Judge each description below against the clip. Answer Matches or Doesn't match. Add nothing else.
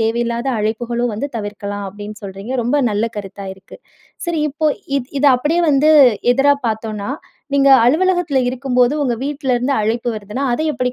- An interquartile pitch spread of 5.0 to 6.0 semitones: Doesn't match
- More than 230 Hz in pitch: Matches